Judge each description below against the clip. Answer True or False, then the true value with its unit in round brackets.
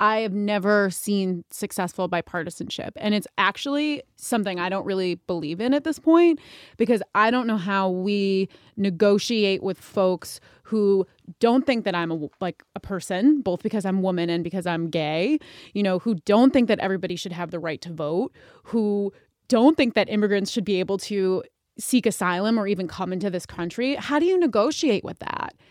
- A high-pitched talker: True (200 Hz)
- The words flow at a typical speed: True (185 wpm)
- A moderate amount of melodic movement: True (3.6 semitones)